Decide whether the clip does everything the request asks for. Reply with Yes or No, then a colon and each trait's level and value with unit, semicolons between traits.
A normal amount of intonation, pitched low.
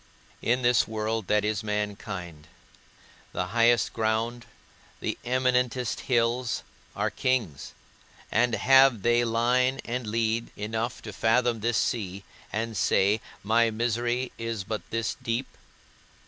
No: narrow, 2.2 semitones; low, 115 Hz